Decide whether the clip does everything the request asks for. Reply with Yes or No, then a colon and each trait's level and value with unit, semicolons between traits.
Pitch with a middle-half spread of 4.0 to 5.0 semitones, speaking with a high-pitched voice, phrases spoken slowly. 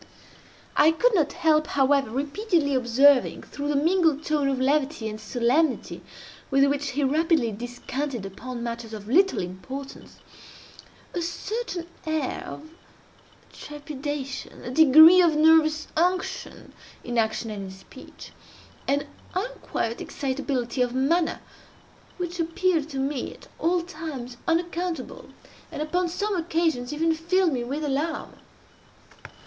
Yes: average, 4.3 semitones; very high, 290 Hz; slow, 120 wpm